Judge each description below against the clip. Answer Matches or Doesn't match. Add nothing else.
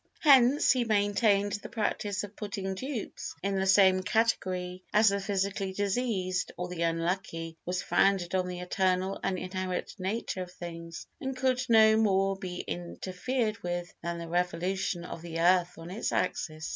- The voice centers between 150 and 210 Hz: Matches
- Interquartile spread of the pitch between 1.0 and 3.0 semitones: Matches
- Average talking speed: Matches